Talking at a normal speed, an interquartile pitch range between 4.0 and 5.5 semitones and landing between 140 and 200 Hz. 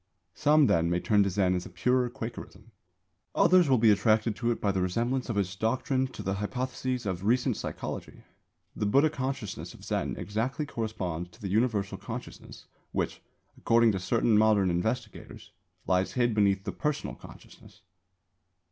No: average, 165 wpm; average, 4.4 semitones; low, 110 Hz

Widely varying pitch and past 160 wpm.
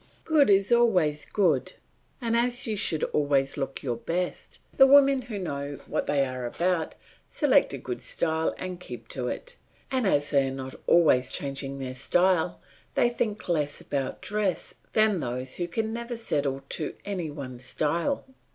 Yes: wide, 7.7 semitones; average, 170 wpm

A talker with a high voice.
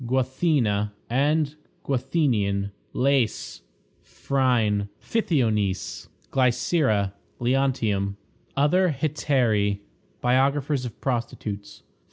No: low, 125 Hz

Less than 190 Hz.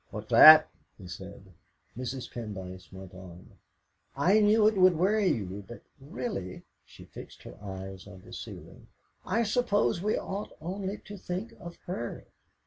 Yes: medium, 140 Hz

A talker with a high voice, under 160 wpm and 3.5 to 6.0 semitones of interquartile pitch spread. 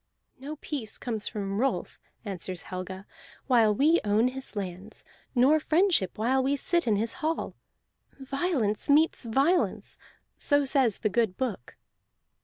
Yes: high, 245 Hz; slow, 135 wpm; wide, 5.5 semitones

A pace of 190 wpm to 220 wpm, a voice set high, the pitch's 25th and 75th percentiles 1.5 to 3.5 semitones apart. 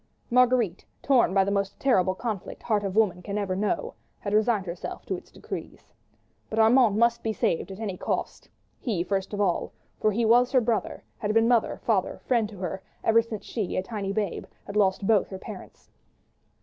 Yes: average, 195 wpm; high, 210 Hz; average, 3.0 semitones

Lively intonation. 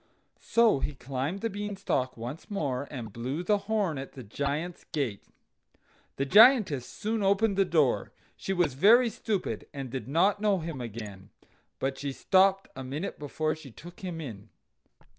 Yes: wide, 6.9 semitones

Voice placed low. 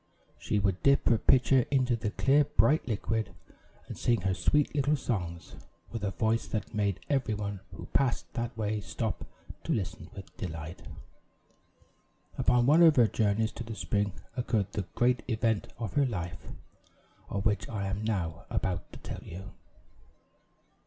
Yes: low, 110 Hz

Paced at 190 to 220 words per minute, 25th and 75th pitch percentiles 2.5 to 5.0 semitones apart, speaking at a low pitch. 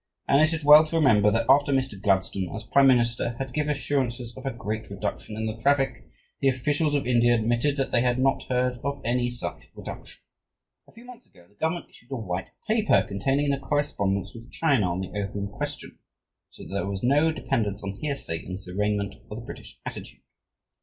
No: fast, 205 wpm; wide, 5.4 semitones; low, 120 Hz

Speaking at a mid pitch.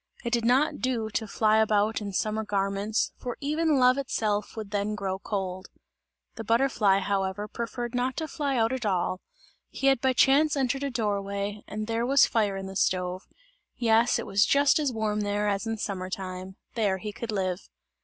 No: high, 215 Hz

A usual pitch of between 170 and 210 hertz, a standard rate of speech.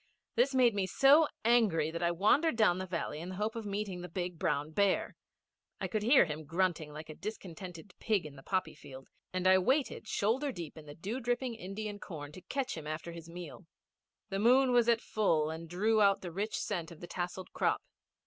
No: medium, 185 Hz; fast, 215 wpm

